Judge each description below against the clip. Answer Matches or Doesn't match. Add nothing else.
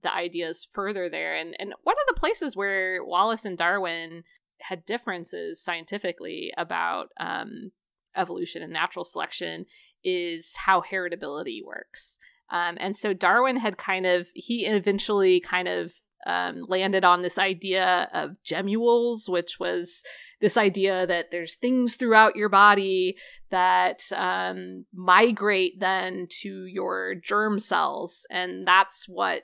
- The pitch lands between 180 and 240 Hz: Matches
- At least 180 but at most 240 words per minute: Doesn't match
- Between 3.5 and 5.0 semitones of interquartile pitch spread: Doesn't match